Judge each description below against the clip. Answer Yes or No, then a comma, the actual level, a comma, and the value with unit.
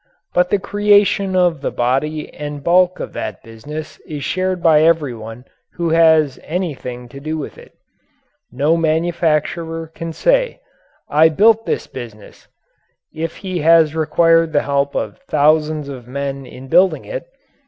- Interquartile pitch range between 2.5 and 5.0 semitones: Yes, average, 3.6 semitones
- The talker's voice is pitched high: No, medium, 155 Hz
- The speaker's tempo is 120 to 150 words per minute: Yes, average, 145 wpm